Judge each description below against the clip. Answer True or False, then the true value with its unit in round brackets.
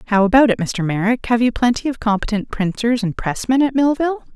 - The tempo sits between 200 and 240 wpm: True (205 wpm)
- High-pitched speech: True (230 Hz)